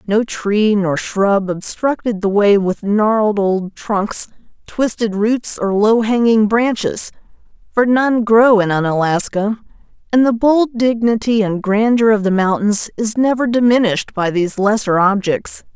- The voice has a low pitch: No, high, 215 Hz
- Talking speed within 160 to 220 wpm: No, average, 145 wpm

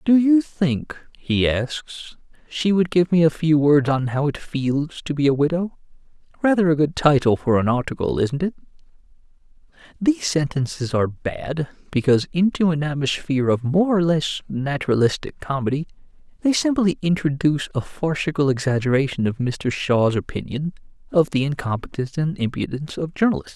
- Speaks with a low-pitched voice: No, medium, 150 Hz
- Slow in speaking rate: No, average, 155 wpm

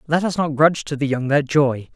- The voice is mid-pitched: Yes, medium, 145 Hz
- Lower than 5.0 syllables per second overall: No, 5.7 syllables/s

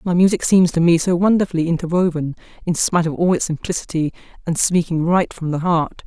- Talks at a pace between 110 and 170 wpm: No, average, 200 wpm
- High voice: No, medium, 170 Hz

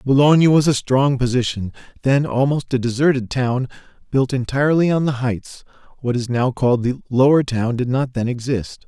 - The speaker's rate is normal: Yes, average, 175 wpm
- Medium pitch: No, low, 130 Hz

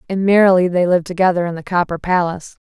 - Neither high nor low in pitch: Yes, medium, 180 Hz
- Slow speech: No, average, 200 wpm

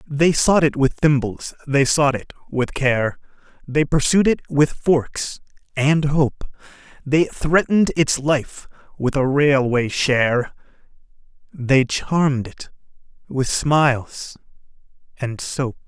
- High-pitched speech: No, medium, 140 Hz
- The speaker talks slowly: Yes, slow, 120 wpm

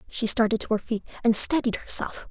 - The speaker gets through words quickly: Yes, fast, 210 wpm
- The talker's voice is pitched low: No, high, 225 Hz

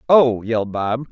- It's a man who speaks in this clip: Yes, male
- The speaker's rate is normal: Yes, average, 160 wpm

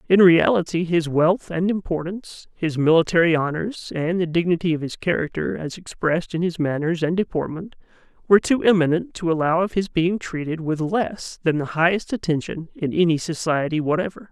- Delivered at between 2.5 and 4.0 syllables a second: No, 5.4 syllables/s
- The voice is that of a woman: No, male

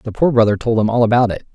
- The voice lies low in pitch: Yes, low, 115 Hz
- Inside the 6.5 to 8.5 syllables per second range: Yes, 6.9 syllables/s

